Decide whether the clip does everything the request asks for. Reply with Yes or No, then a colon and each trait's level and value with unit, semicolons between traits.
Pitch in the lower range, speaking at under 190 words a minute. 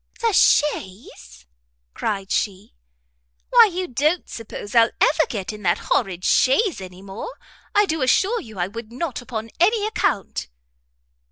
No: high, 235 Hz; average, 145 wpm